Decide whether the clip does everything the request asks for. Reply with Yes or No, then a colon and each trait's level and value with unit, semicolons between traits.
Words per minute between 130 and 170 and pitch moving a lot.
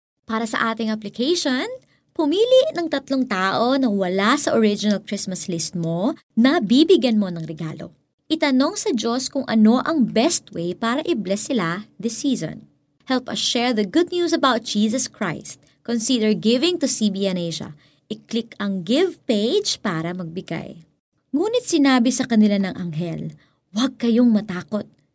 Yes: average, 150 wpm; wide, 6.0 semitones